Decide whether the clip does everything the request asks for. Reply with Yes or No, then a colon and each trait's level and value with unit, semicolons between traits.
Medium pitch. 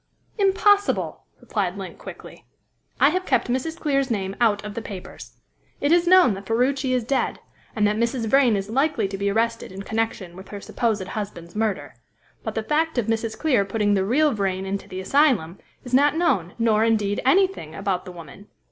No: high, 225 Hz